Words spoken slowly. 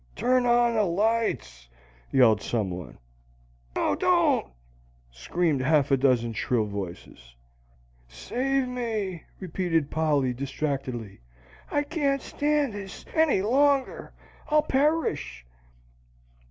Yes: slow, 100 wpm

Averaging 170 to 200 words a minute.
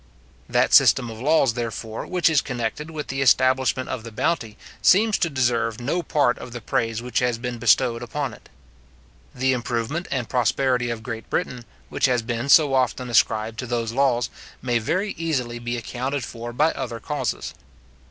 Yes: average, 175 wpm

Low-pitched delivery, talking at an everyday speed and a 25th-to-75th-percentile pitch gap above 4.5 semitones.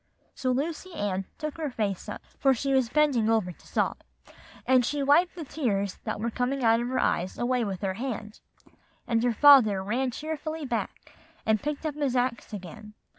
No: high, 245 Hz; average, 190 wpm; average, 4.9 semitones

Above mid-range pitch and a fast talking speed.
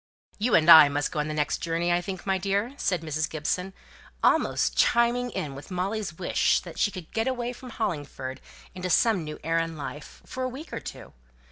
No: medium, 180 Hz; fast, 210 wpm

